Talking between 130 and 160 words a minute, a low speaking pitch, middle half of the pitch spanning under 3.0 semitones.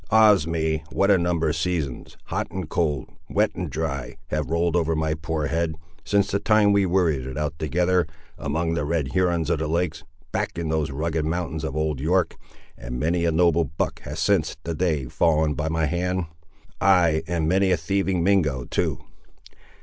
No: average, 190 wpm; very low, 80 Hz; narrow, 2.5 semitones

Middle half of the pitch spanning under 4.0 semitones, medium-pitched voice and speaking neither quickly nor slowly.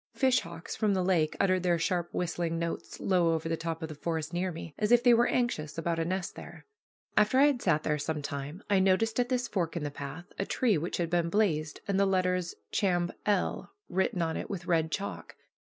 No: average, 3.4 semitones; medium, 175 Hz; fast, 230 wpm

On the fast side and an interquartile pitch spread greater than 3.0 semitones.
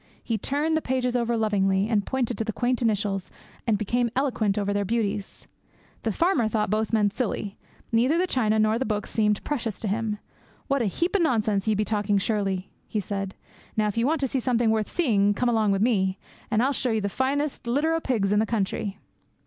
Yes: fast, 215 wpm; average, 3.4 semitones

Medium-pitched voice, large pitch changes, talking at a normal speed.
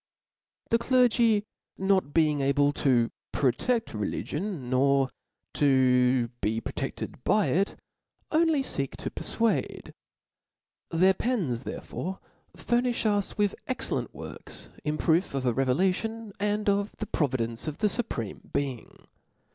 No: medium, 170 Hz; wide, 8.3 semitones; slow, 120 wpm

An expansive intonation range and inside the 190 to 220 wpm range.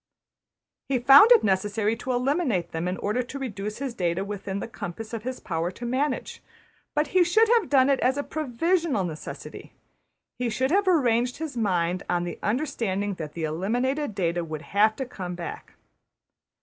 No: wide, 6.6 semitones; average, 175 wpm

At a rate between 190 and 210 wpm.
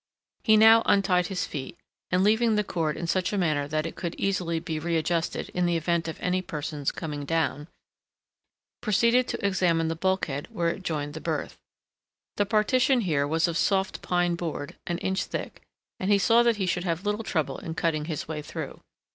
Yes: average, 195 wpm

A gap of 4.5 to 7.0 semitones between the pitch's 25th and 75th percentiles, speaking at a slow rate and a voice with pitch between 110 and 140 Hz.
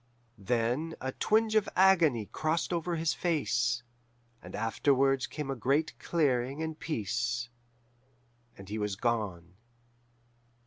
Yes: wide, 5.5 semitones; slow, 120 wpm; low, 135 Hz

